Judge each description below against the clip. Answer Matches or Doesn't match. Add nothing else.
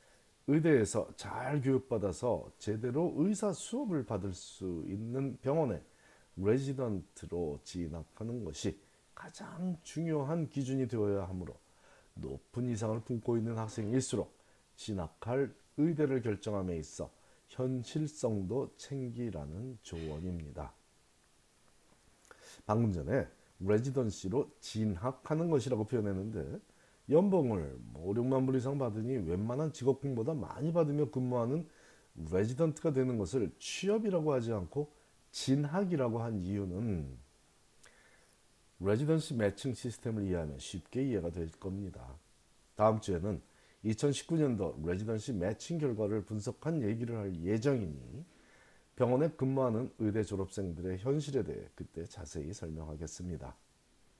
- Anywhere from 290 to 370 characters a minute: Doesn't match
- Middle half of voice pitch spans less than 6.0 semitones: Doesn't match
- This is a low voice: Matches